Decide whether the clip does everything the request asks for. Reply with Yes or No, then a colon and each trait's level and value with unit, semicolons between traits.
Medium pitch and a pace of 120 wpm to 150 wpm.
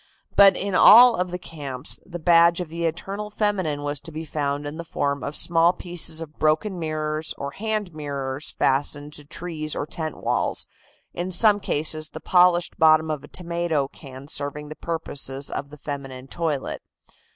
No: medium, 155 Hz; average, 175 wpm